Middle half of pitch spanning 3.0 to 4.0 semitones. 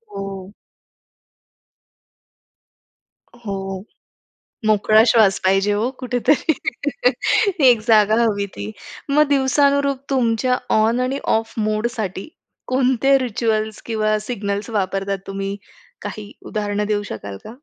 Yes: average, 3.6 semitones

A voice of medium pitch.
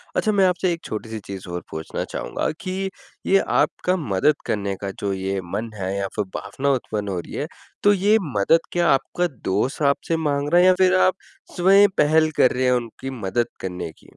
No: low, 130 Hz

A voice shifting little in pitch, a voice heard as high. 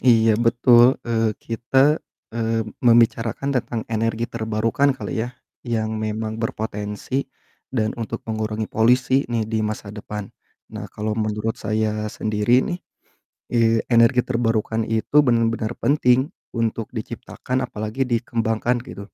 No: narrow, 1.9 semitones; low, 115 Hz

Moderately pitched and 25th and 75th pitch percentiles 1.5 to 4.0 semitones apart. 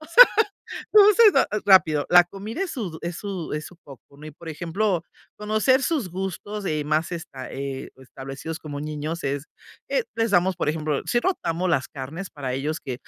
No: medium, 165 Hz; wide, 5.5 semitones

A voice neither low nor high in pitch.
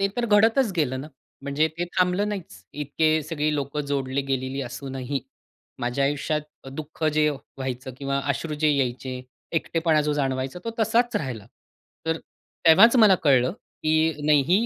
Yes: medium, 150 Hz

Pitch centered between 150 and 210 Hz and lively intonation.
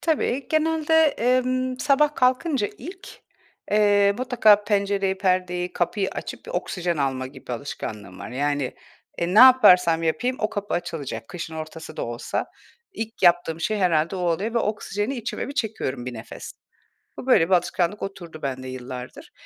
Yes: high, 190 Hz; wide, 7.1 semitones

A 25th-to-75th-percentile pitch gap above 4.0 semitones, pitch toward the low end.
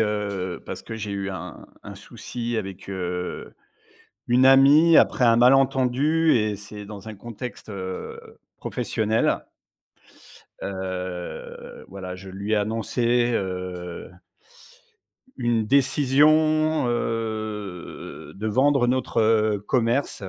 Yes: average, 4.4 semitones; low, 110 Hz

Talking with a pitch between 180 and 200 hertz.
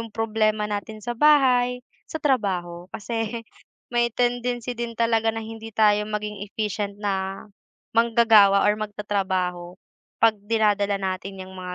No: high, 215 Hz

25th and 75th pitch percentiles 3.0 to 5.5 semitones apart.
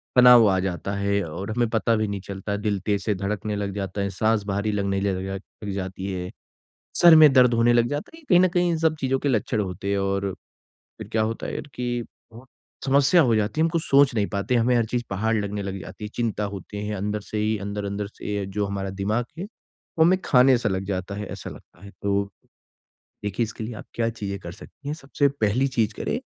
Yes: average, 3.5 semitones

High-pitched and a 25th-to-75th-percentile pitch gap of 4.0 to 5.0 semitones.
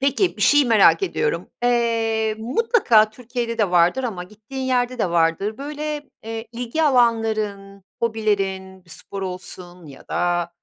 Yes: high, 225 Hz; average, 4.4 semitones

